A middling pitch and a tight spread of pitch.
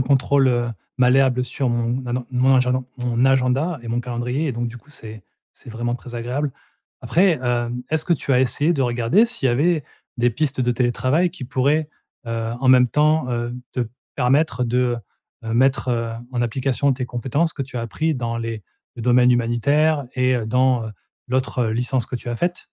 No: low, 125 Hz; narrow, 2.3 semitones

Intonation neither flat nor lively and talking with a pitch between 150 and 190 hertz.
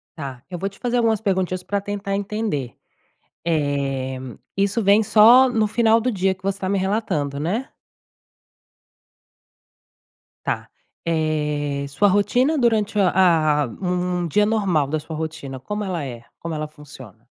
No: wide, 5.7 semitones; medium, 185 Hz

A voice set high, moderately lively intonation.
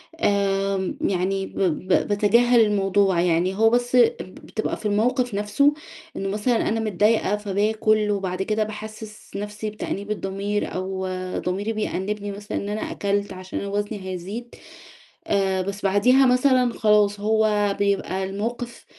No: high, 205 Hz; narrow, 1.9 semitones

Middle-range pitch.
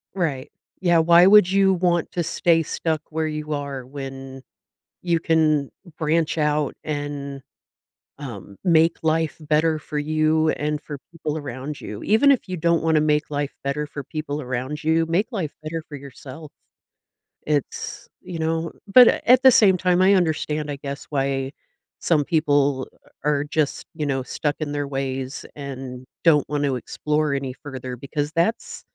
Yes: medium, 150 Hz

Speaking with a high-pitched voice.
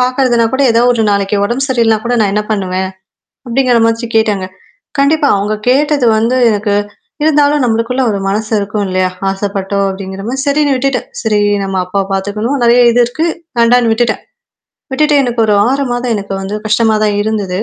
Yes: high, 230 Hz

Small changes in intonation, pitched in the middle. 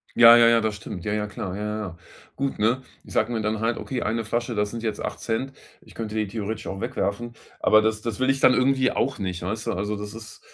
No: narrow, 2.2 semitones; low, 110 Hz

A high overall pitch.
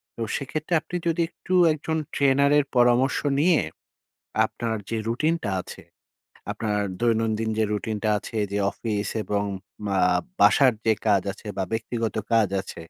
No: low, 115 Hz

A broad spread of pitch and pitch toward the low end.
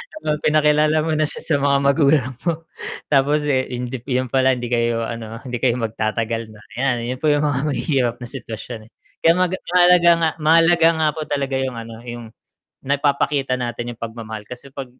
No: average, 4.2 semitones; low, 130 Hz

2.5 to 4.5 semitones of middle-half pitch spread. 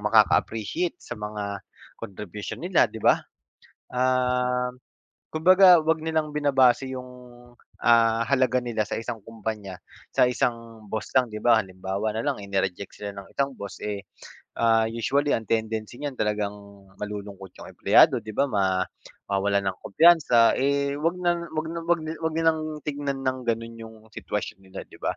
No: average, 5.1 semitones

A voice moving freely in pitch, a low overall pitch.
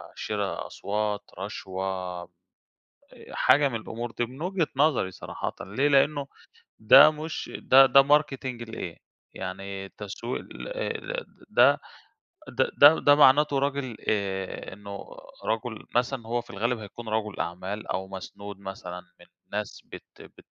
Yes: wide, 5.9 semitones; low, 115 Hz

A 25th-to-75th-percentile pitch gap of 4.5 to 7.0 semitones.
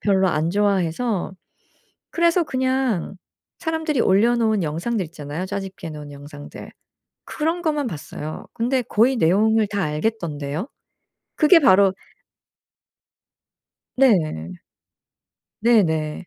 No: wide, 7.4 semitones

